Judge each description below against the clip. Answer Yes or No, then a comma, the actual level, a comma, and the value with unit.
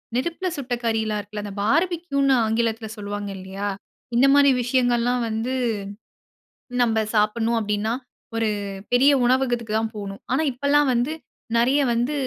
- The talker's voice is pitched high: Yes, high, 235 Hz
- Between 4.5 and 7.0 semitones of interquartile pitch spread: No, average, 3.6 semitones